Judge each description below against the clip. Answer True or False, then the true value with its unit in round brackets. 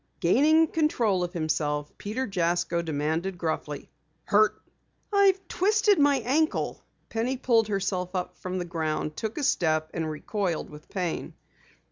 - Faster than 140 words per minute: False (135 wpm)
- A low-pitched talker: False (185 Hz)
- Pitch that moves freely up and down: True (8.0 semitones)